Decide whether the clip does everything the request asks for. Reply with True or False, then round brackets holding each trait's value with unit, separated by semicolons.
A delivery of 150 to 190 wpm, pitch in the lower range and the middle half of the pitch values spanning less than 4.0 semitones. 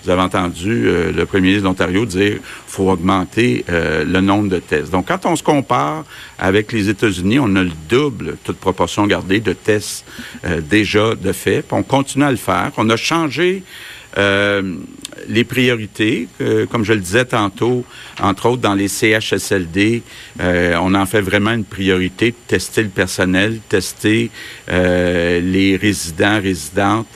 True (170 wpm; 100 Hz; 3.4 semitones)